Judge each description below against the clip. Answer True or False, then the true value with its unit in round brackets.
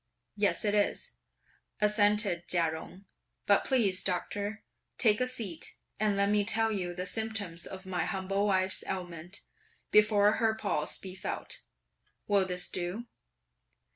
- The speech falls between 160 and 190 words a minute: False (140 wpm)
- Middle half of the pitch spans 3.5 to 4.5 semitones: False (2.5 semitones)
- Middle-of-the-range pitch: False (200 Hz)